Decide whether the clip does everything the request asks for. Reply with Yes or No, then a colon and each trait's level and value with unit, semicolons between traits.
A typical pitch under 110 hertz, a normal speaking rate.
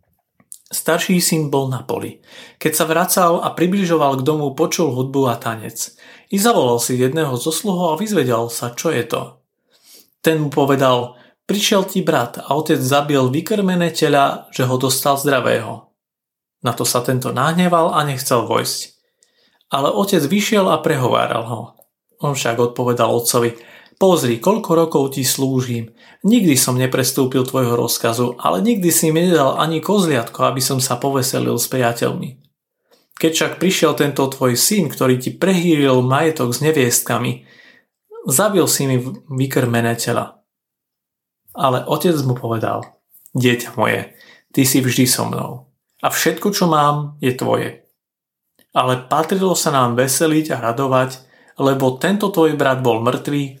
No: medium, 140 Hz; average, 145 wpm